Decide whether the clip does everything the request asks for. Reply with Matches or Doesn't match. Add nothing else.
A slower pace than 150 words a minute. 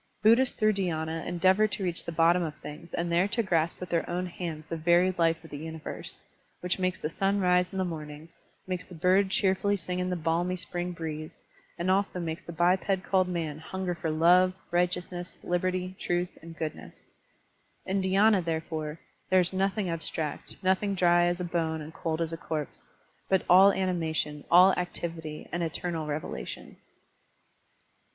Doesn't match